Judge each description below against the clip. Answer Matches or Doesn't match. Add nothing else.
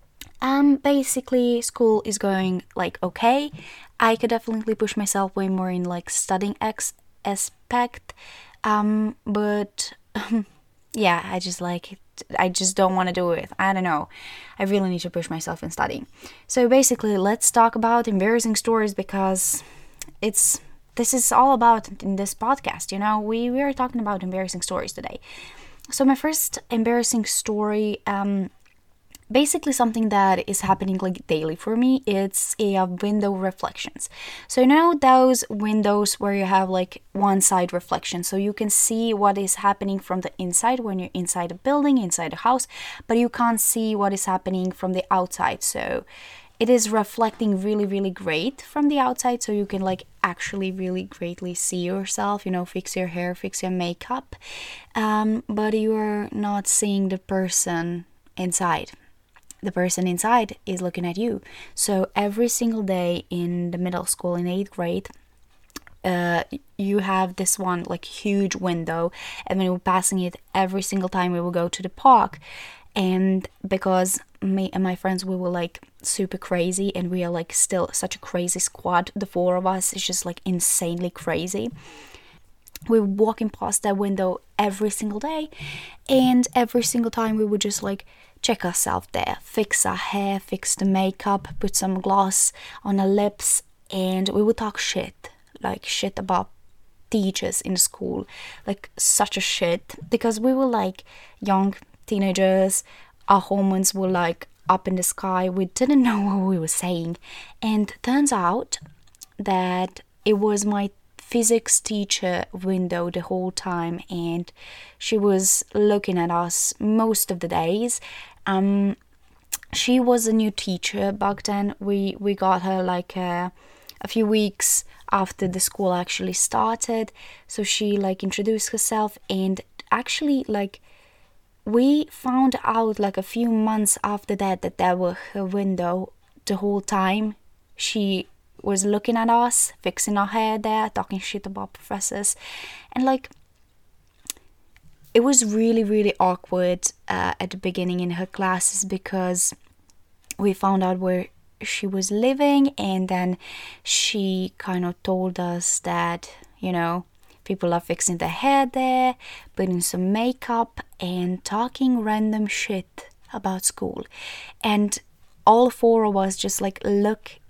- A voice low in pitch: Doesn't match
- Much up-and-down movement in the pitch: Doesn't match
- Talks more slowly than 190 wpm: Matches